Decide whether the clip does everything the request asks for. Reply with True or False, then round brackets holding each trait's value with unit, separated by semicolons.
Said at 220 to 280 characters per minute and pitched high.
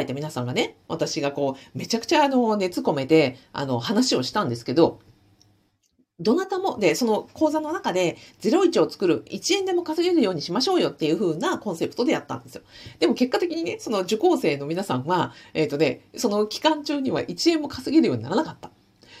False (400 characters per minute; 215 Hz)